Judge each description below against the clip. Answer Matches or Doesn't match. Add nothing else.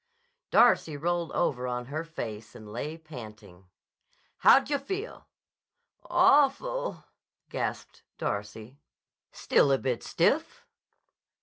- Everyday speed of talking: Doesn't match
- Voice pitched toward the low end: Doesn't match